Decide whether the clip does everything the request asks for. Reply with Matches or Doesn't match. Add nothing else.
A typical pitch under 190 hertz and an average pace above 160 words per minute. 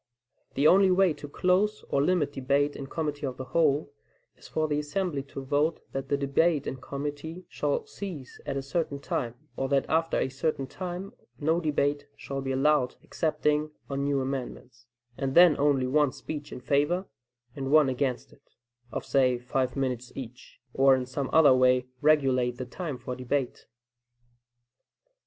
Matches